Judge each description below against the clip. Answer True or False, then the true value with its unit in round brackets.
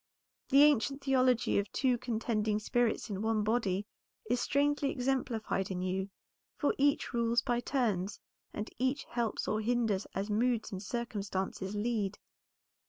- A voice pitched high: True (230 Hz)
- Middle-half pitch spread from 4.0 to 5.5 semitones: False (3.4 semitones)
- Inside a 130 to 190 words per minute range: True (140 wpm)